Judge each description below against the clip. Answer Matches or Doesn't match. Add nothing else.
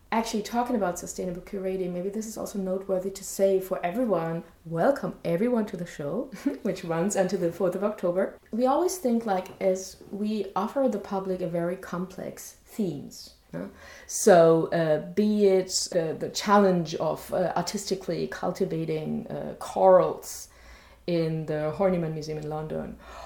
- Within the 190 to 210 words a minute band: Doesn't match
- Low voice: Doesn't match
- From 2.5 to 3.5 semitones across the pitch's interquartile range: Matches